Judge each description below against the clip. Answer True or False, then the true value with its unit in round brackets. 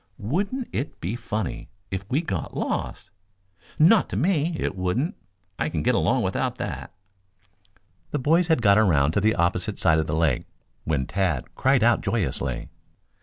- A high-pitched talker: False (105 Hz)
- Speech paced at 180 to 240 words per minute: False (165 wpm)